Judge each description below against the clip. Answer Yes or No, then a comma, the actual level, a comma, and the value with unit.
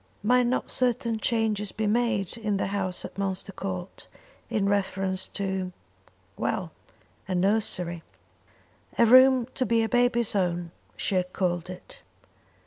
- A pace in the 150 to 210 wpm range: No, slow, 135 wpm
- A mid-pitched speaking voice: No, high, 200 Hz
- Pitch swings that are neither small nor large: Yes, average, 3.9 semitones